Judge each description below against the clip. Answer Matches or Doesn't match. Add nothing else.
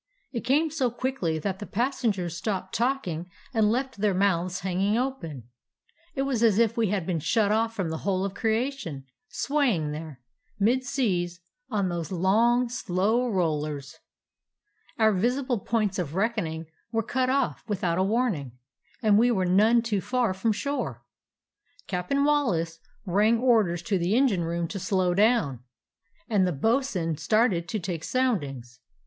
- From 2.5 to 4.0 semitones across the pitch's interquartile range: Doesn't match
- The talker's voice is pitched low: Doesn't match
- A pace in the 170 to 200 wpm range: Doesn't match